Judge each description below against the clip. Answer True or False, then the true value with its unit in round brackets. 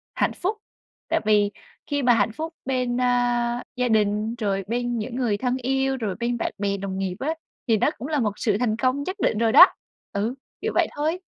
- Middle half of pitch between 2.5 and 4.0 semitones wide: True (3.6 semitones)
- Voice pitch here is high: True (240 Hz)